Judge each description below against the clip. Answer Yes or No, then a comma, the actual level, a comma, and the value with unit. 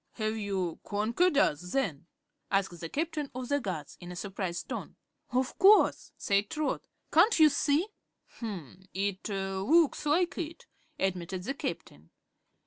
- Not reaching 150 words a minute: Yes, slow, 135 wpm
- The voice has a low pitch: No, high, 205 Hz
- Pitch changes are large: Yes, wide, 7.5 semitones